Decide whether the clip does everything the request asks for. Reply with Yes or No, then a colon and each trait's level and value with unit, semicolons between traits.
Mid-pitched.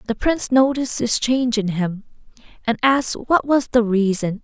No: high, 235 Hz